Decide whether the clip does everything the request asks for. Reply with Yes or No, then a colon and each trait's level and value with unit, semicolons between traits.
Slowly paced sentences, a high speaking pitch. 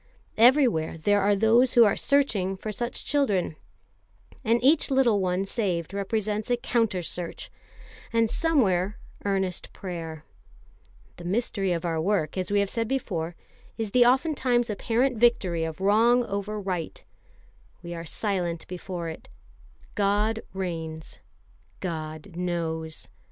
Yes: slow, 130 wpm; high, 200 Hz